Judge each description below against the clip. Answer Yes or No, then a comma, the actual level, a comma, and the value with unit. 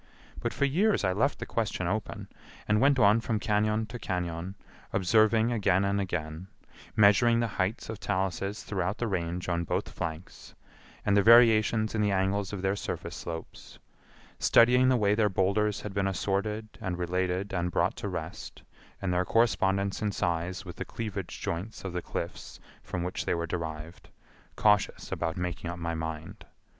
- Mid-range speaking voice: No, low, 100 Hz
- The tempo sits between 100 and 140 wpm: No, average, 170 wpm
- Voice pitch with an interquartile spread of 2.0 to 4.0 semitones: Yes, average, 3.3 semitones